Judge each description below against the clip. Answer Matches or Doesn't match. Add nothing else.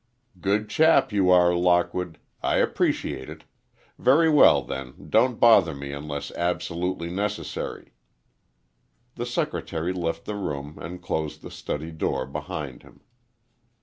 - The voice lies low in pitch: Matches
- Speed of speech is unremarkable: Doesn't match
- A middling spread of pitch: Matches